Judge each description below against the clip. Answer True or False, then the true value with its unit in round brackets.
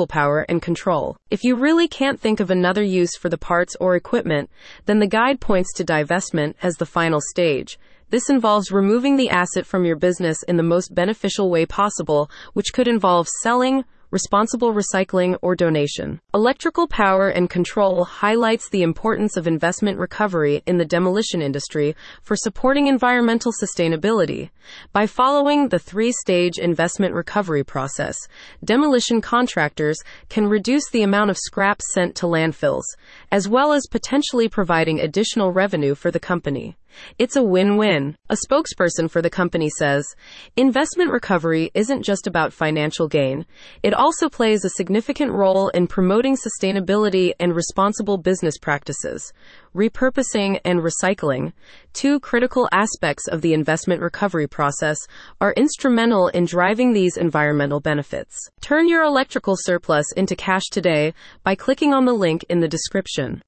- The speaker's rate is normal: True (150 wpm)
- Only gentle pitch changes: False (5.0 semitones)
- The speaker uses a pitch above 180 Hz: True (190 Hz)